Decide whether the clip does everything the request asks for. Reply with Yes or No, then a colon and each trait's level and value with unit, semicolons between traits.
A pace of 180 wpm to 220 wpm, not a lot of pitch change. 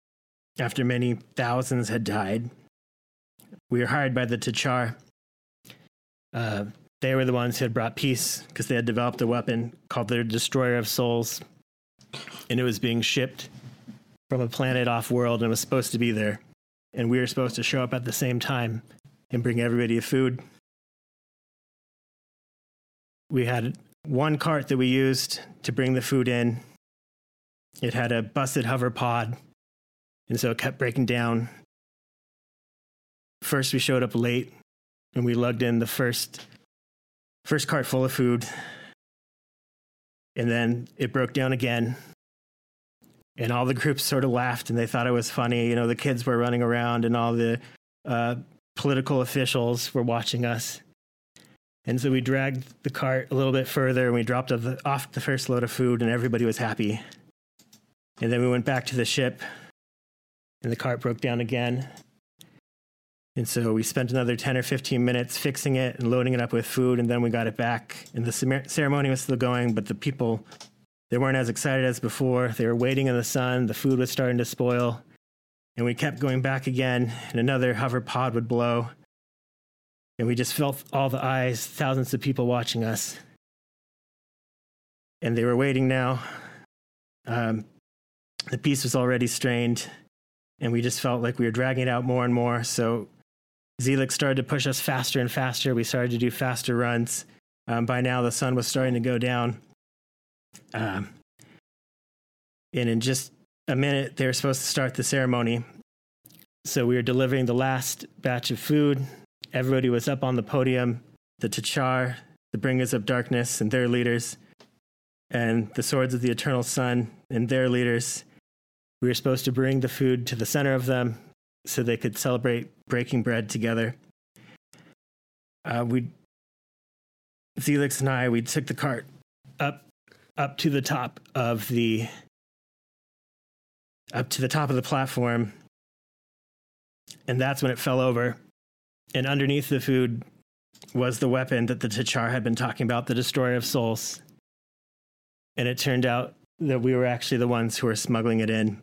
No: average, 170 wpm; narrow, 1.9 semitones